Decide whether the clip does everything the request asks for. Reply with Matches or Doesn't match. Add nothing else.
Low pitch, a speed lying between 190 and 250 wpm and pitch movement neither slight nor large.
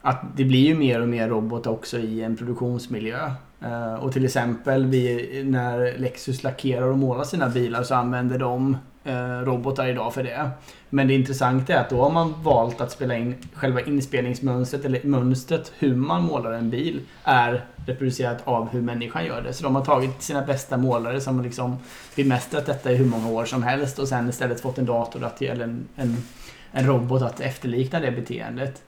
Doesn't match